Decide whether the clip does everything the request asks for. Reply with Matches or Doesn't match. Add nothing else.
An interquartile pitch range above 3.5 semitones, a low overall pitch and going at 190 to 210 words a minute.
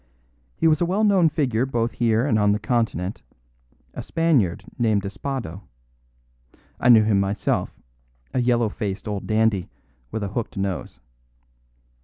Doesn't match